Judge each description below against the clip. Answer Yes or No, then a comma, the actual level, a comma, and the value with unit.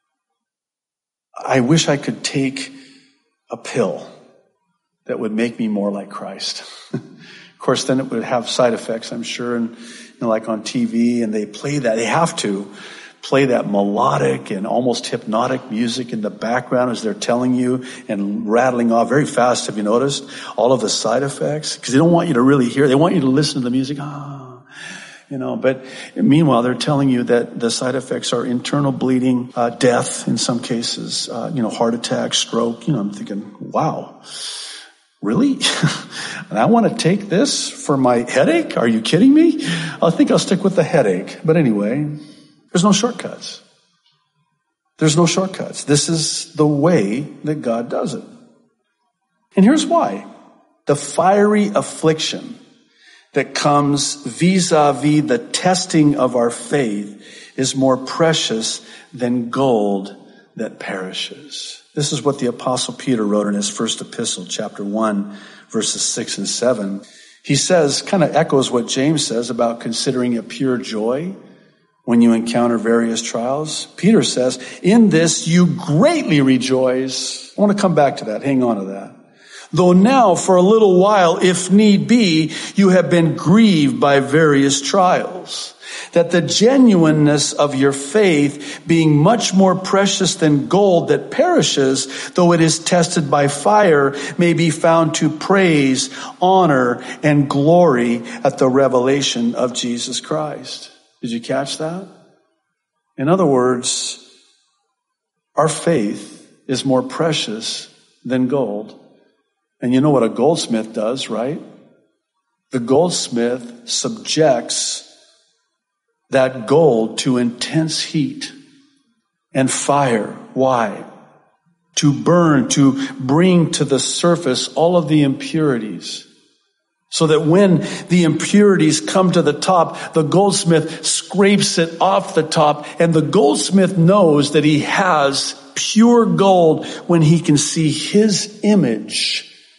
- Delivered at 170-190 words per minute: No, average, 150 wpm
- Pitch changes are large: Yes, wide, 5.9 semitones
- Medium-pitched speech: Yes, medium, 150 Hz